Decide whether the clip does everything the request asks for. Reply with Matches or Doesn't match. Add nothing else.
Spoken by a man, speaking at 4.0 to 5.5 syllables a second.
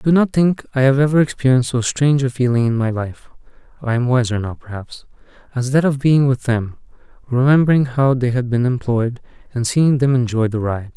Matches